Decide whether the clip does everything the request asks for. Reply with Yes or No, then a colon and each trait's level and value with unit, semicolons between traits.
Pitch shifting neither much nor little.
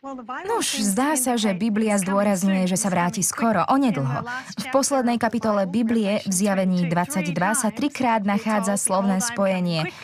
Yes: average, 3.9 semitones